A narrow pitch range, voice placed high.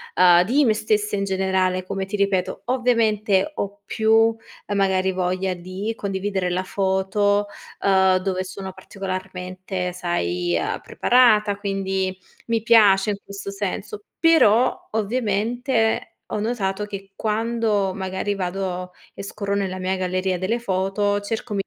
Yes: narrow, 2.2 semitones; high, 195 Hz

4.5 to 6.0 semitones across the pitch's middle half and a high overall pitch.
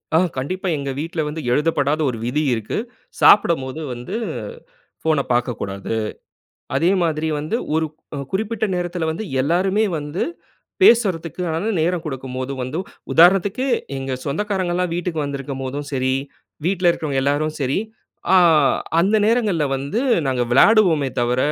No: average, 5.0 semitones; medium, 160 Hz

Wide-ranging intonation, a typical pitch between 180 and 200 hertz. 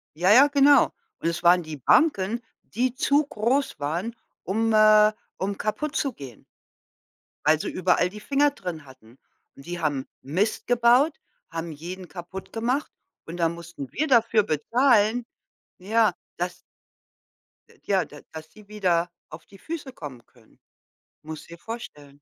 Yes: wide, 6.5 semitones; high, 190 Hz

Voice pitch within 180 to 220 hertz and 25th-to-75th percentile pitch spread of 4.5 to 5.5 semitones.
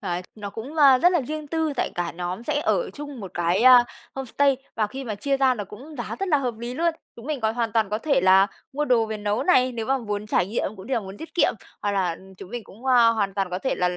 No: high, 235 Hz; average, 5.2 semitones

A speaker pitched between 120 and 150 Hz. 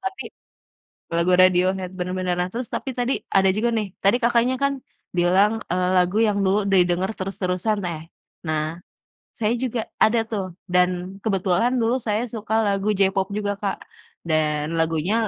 No: high, 195 Hz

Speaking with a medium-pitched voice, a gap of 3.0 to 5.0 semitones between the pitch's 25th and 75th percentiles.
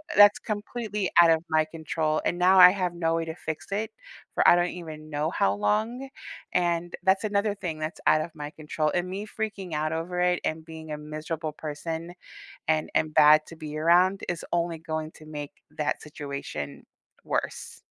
No: medium, 165 Hz; narrow, 2.6 semitones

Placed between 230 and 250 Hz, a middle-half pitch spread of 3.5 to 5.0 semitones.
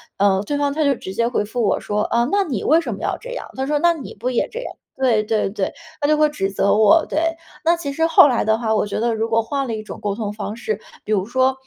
No: high, 235 Hz; wide, 5.4 semitones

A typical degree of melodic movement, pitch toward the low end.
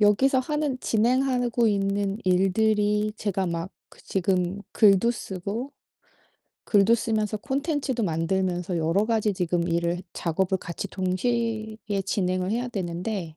No: average, 3.9 semitones; high, 200 Hz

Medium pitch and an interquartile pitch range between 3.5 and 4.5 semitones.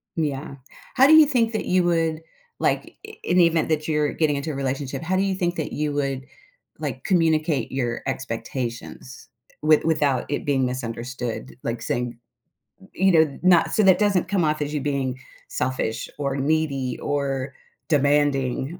Yes: medium, 145 Hz; average, 4.0 semitones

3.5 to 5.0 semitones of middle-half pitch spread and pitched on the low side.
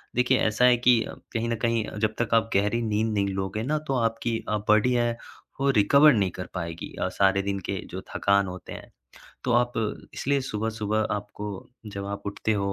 No: average, 2.8 semitones; low, 110 Hz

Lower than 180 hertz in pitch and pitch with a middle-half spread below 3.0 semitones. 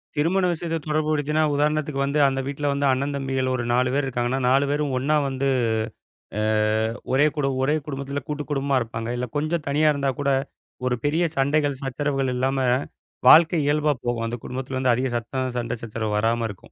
Yes: medium, 140 Hz; narrow, 2.5 semitones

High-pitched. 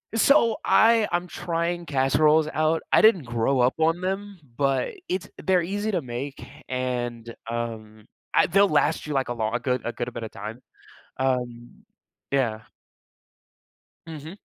No: medium, 140 Hz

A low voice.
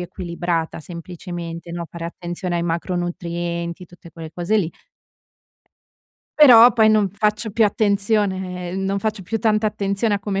No: medium, 185 Hz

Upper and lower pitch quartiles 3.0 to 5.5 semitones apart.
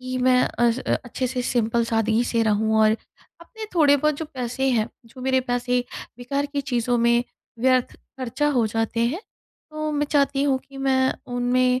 No: narrow, 2.6 semitones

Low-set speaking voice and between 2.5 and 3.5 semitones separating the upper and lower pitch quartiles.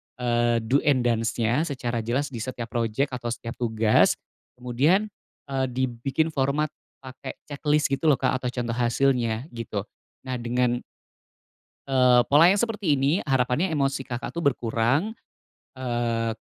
Yes: low, 125 Hz; average, 2.8 semitones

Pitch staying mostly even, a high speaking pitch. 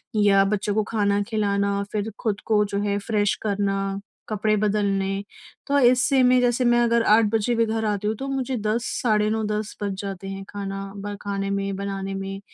Yes: narrow, 1.9 semitones; high, 205 Hz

